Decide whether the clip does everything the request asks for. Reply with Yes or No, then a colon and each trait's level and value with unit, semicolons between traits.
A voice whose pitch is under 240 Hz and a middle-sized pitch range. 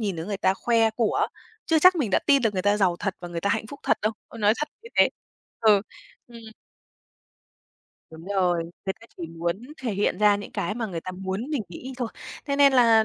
Yes: high, 210 Hz; average, 4.3 semitones